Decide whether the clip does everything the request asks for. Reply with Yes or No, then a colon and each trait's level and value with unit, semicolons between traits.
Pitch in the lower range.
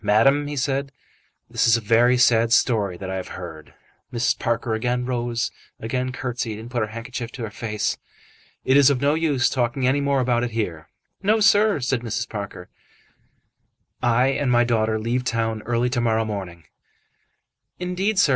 Yes: low, 120 Hz